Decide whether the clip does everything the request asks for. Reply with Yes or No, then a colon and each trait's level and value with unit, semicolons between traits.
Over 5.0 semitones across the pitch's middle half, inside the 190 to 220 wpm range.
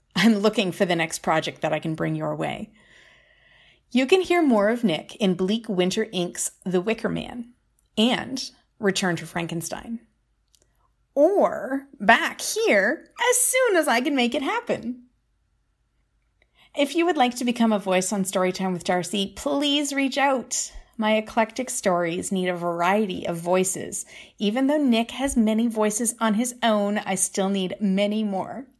No: wide, 5.4 semitones; average, 160 wpm